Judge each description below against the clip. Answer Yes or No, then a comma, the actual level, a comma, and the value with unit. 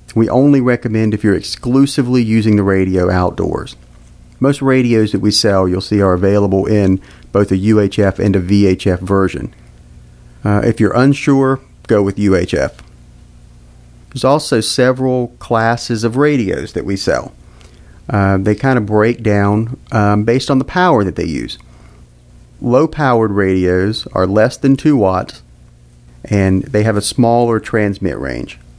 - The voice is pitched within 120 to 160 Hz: No, low, 105 Hz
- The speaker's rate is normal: Yes, average, 150 wpm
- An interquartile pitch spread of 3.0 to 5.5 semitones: Yes, average, 4.4 semitones